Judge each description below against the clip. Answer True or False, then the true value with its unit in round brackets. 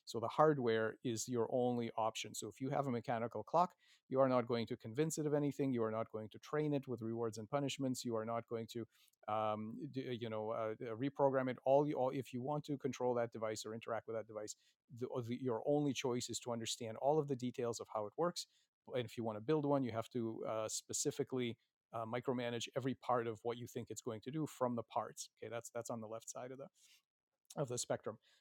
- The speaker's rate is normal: False (245 wpm)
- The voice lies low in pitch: True (120 Hz)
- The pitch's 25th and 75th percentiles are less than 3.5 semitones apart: True (3.1 semitones)